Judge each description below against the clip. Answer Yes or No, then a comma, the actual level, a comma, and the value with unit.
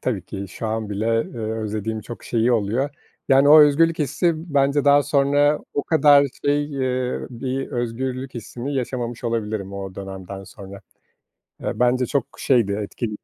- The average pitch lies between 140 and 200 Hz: No, low, 125 Hz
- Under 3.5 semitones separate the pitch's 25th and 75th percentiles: No, average, 4.5 semitones